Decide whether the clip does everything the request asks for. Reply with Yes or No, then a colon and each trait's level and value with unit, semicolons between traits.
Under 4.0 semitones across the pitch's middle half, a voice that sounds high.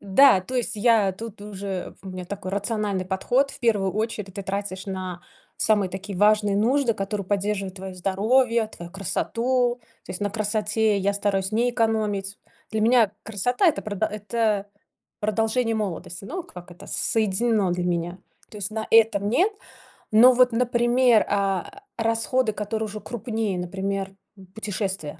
Yes: average, 2.9 semitones; high, 210 Hz